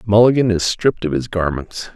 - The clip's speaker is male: Yes, male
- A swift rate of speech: No, average, 185 wpm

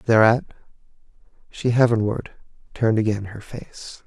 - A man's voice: Yes, male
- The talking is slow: Yes, slow, 105 wpm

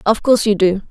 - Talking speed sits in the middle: No, fast, 265 wpm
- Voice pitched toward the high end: Yes, high, 205 Hz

